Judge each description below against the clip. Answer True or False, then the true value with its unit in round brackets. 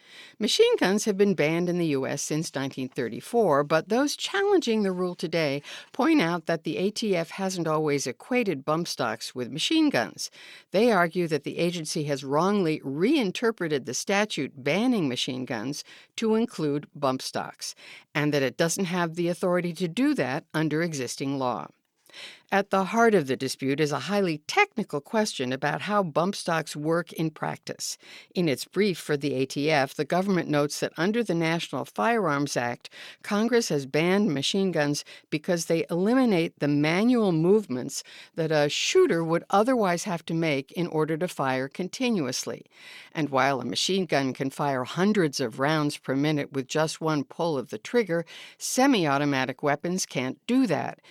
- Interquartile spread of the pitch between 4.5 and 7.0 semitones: True (5.5 semitones)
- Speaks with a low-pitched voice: False (165 Hz)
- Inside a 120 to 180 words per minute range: True (165 wpm)